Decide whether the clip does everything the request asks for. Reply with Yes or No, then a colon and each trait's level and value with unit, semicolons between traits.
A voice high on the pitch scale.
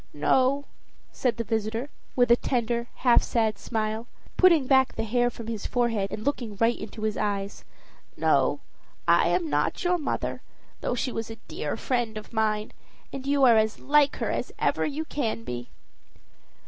Yes: high, 235 Hz